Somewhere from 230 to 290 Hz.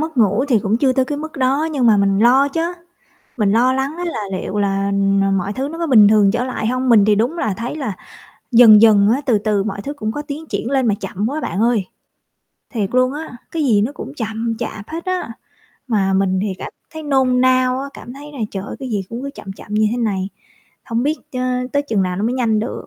Yes: high, 235 Hz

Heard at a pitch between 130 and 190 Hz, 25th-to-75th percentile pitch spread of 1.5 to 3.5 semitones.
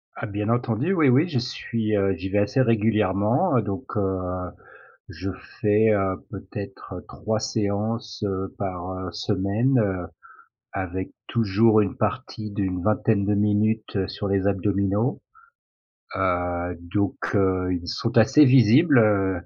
No: low, 105 Hz; average, 2.9 semitones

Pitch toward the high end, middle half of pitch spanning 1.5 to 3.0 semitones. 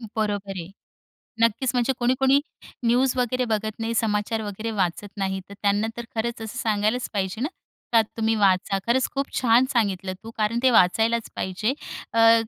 Yes: high, 225 Hz; narrow, 2.6 semitones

